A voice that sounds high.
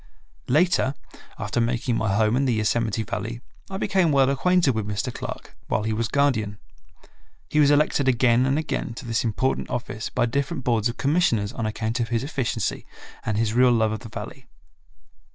No: low, 120 Hz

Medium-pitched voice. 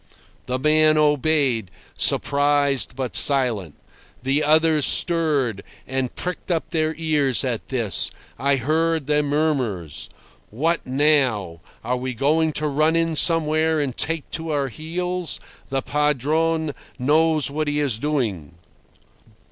Yes: medium, 145 Hz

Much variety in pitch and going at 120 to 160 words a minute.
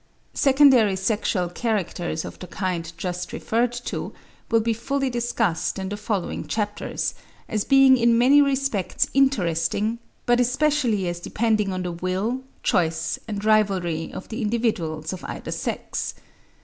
No: average, 4.9 semitones; average, 140 wpm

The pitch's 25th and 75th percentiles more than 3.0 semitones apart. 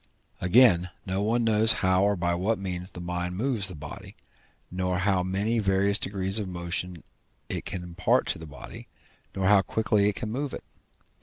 No: average, 2.7 semitones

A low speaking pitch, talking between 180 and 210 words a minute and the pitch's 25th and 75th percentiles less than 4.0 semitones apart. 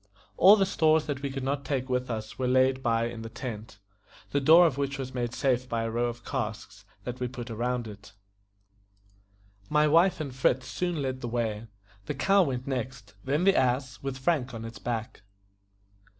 Yes: low, 130 Hz; average, 195 wpm; average, 3.0 semitones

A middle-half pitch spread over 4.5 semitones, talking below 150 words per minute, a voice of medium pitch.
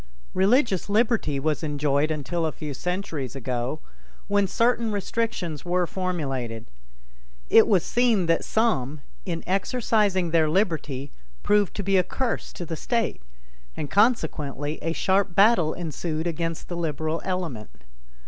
Yes: average, 4.9 semitones; slow, 135 wpm; medium, 175 Hz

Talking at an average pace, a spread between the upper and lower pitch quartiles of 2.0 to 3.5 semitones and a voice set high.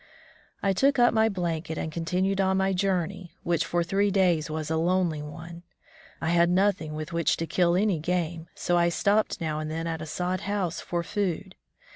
No: average, 195 wpm; average, 2.9 semitones; medium, 175 Hz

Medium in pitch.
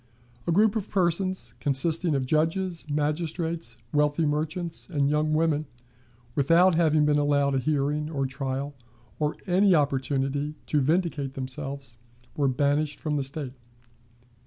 Yes: medium, 150 Hz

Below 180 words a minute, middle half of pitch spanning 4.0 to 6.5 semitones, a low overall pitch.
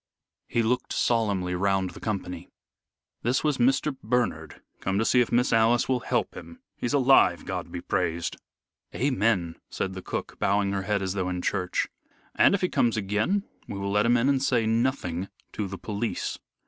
No: average, 185 wpm; average, 4.3 semitones; low, 110 Hz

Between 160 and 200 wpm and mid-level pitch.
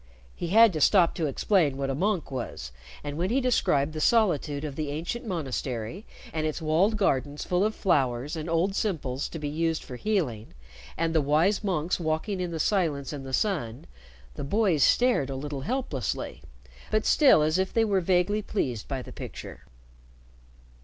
Yes: average, 180 wpm; medium, 160 Hz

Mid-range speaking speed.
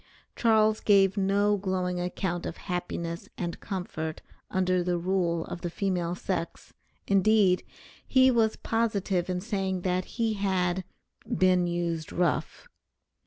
No: slow, 125 wpm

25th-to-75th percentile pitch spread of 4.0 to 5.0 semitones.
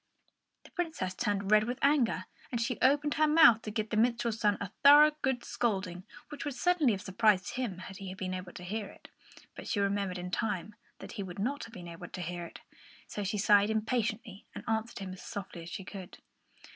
Yes: average, 4.3 semitones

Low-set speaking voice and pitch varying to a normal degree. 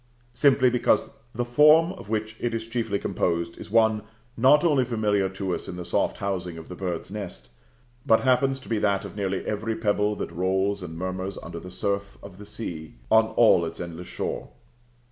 Yes: low, 105 Hz; average, 3.8 semitones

